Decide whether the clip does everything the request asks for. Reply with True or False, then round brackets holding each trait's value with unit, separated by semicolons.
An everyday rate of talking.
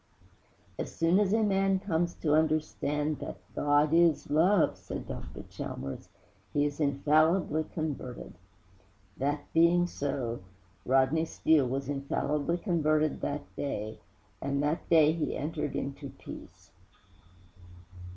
False (120 wpm)